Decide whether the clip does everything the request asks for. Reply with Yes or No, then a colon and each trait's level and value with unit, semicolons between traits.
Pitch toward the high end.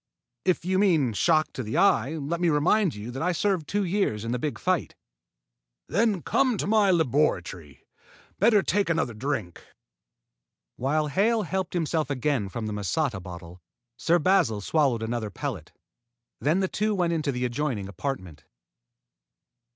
No: medium, 150 Hz